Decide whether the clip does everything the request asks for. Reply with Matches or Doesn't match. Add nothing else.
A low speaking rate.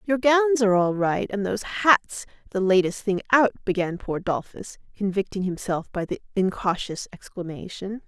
Doesn't match